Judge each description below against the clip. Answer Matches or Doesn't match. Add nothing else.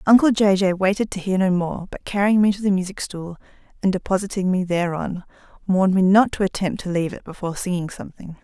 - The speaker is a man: Doesn't match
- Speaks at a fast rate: Matches